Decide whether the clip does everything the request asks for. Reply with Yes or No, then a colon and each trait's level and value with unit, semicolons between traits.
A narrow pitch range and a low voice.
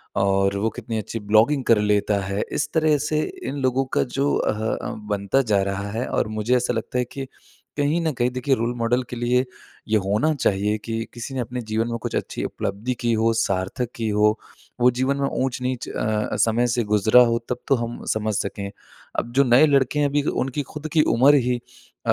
No: average, 3.4 semitones; low, 120 Hz